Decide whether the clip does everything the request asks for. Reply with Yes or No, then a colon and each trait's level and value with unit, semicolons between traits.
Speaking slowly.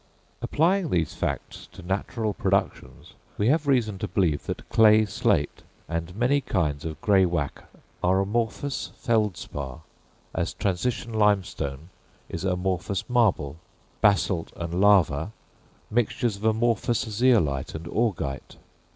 Yes: slow, 115 wpm